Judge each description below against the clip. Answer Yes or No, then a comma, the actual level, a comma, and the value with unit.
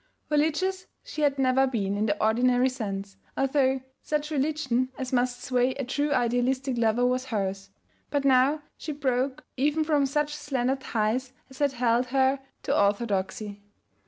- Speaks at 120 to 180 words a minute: Yes, average, 155 wpm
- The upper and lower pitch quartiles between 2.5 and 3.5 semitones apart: Yes, average, 3.0 semitones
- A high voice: Yes, very high, 255 Hz